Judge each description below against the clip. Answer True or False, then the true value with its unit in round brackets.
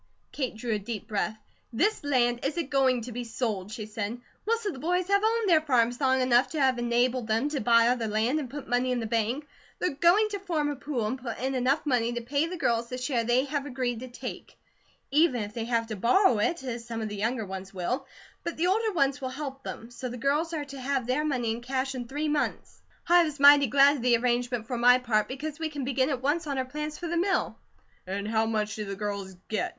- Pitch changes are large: False (3.9 semitones)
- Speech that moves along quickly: True (250 wpm)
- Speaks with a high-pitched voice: True (255 Hz)